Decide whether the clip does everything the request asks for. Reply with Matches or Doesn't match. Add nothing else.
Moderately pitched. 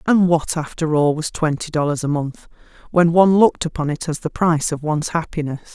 Matches